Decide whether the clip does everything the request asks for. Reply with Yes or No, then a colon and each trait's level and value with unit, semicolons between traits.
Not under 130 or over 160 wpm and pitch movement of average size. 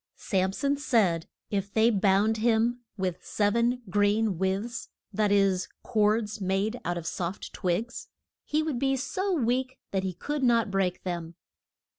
Yes: average, 155 wpm; average, 4.0 semitones